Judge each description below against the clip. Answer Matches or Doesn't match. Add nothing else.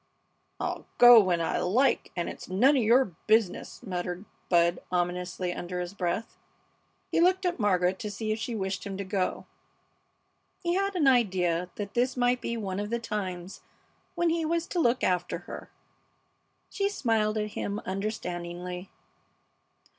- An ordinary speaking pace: Matches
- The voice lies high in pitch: Matches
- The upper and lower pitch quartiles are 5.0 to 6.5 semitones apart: Matches